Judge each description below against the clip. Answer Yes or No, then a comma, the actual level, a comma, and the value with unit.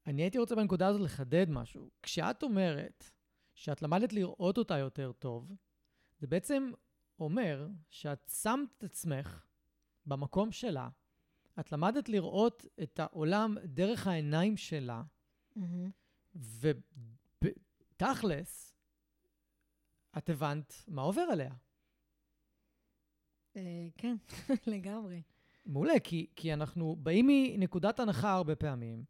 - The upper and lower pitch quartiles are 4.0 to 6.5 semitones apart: Yes, wide, 5.4 semitones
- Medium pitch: Yes, medium, 170 Hz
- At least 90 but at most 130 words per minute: Yes, slow, 100 wpm